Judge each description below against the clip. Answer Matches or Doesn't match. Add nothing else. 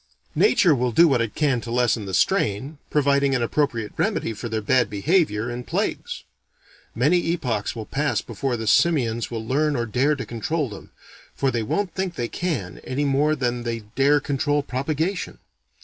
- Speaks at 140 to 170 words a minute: Doesn't match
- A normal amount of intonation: Matches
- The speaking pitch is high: Doesn't match